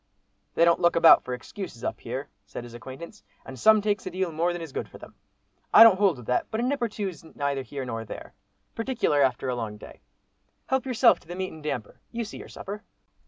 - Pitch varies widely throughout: Yes, wide, 8.0 semitones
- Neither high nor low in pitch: Yes, medium, 170 Hz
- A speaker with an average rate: No, fast, 240 wpm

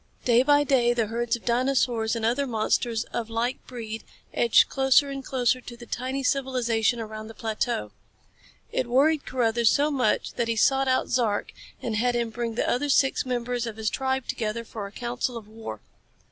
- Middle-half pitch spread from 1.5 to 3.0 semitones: Yes, narrow, 2.4 semitones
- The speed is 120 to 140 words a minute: No, average, 190 wpm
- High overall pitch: Yes, high, 240 Hz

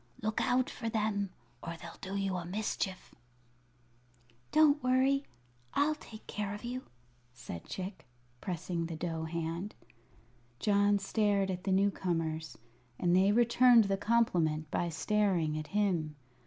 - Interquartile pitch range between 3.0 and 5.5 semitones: Yes, average, 4.4 semitones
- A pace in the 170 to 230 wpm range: No, average, 140 wpm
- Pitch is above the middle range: Yes, high, 195 Hz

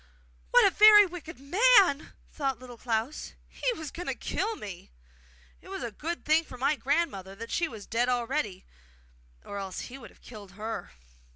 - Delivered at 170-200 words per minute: Yes, average, 180 wpm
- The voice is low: No, very high, 265 Hz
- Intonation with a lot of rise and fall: Yes, wide, 6.8 semitones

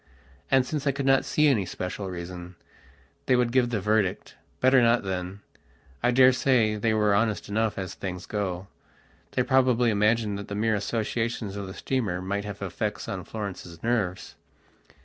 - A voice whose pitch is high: No, low, 105 Hz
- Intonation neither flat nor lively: Yes, average, 4.1 semitones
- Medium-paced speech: Yes, average, 170 wpm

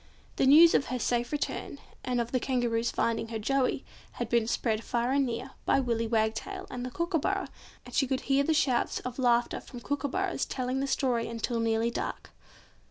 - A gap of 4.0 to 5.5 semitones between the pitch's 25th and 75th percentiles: No, average, 2.8 semitones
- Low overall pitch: No, very high, 250 Hz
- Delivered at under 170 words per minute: No, average, 190 wpm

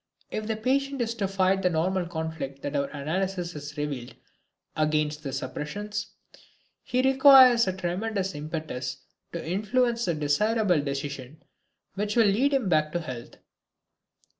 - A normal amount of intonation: No, wide, 6.3 semitones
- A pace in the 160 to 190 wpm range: No, average, 140 wpm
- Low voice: No, medium, 180 Hz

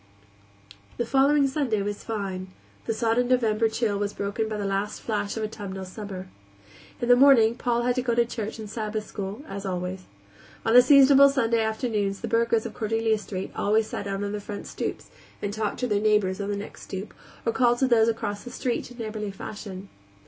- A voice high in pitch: Yes, high, 220 Hz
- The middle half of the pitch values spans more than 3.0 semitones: No, average, 2.7 semitones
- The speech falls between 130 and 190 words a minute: No, average, 200 wpm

